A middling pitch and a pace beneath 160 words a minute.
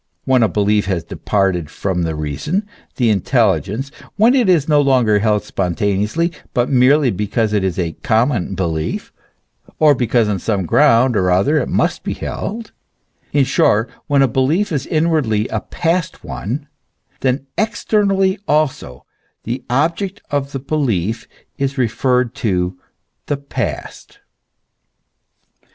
No: low, 125 Hz; average, 140 wpm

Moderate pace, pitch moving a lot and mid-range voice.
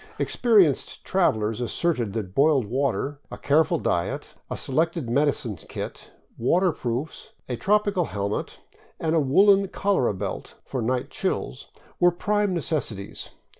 No: slow, 125 wpm; wide, 7.3 semitones; medium, 145 Hz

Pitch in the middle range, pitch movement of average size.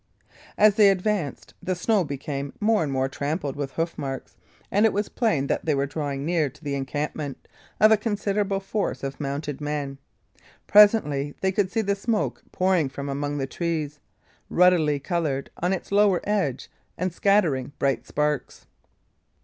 No: medium, 155 Hz; wide, 5.9 semitones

